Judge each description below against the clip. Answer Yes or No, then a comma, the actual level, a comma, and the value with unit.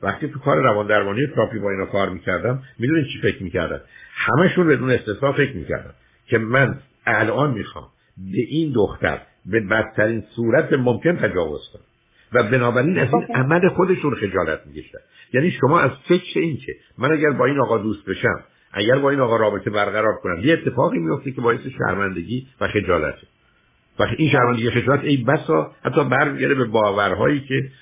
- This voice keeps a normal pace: No, fast, 170 wpm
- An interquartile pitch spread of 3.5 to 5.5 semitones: Yes, average, 5.1 semitones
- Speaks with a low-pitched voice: Yes, low, 130 Hz